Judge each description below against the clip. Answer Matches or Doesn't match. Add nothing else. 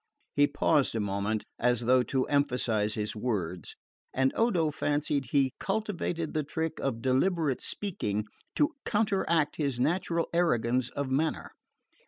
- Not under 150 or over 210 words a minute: Doesn't match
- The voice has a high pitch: Doesn't match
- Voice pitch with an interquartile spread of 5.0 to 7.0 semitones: Matches